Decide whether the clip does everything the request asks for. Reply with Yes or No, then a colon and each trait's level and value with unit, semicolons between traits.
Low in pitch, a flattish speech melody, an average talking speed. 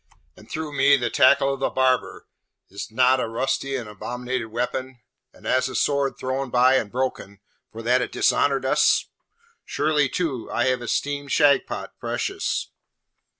Yes: low, 130 Hz; narrow, 1.9 semitones; average, 155 wpm